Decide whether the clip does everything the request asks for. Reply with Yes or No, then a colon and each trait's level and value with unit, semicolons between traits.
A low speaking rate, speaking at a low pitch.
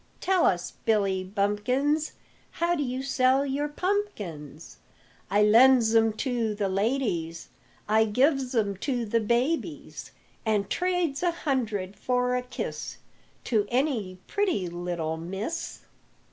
No: slow, 125 wpm; high, 235 Hz